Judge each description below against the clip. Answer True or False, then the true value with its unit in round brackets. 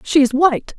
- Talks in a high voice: True (285 Hz)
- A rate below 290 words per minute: True (230 wpm)